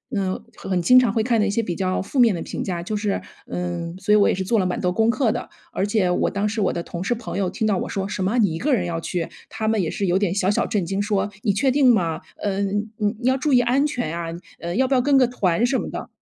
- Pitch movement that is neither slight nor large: Yes, average, 4.4 semitones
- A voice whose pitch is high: Yes, high, 205 Hz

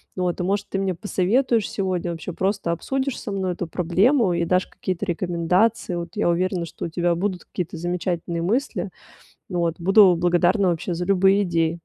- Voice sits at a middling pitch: Yes, medium, 180 Hz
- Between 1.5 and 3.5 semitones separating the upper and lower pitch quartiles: Yes, narrow, 2.4 semitones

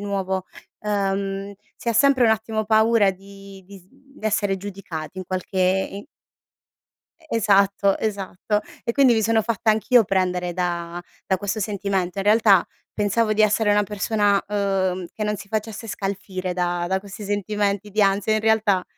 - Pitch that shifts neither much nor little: No, narrow, 2.2 semitones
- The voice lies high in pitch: Yes, high, 200 Hz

